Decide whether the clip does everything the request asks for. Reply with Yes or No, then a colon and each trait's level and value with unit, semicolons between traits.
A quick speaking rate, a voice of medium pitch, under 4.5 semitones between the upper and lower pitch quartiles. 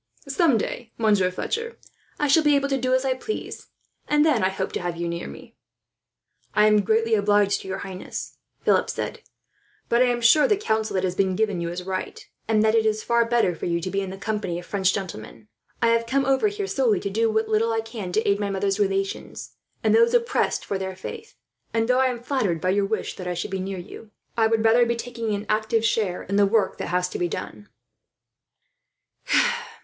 No: fast, 225 wpm; high, 215 Hz; average, 3.8 semitones